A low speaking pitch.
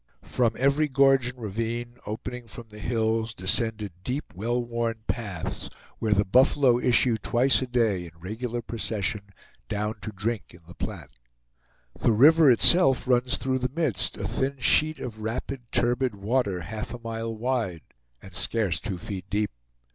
Yes: low, 115 Hz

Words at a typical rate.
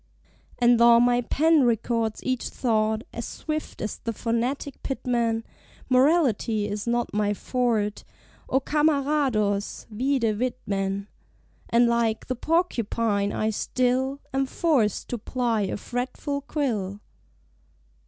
No: slow, 115 wpm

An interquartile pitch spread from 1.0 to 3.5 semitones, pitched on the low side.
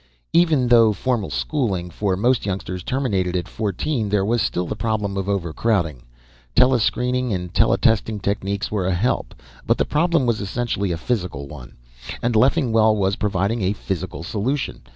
No: average, 4.6 semitones; low, 105 Hz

